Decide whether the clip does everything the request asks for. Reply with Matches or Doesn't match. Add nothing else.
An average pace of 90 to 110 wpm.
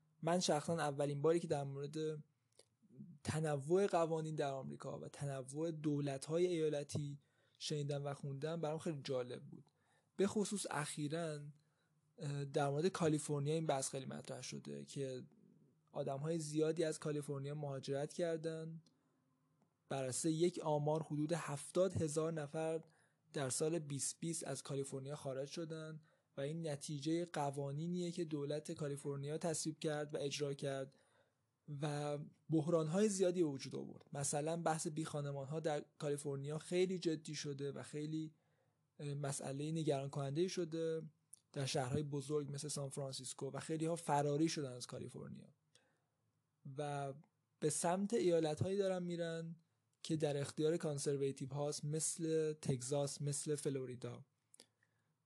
Doesn't match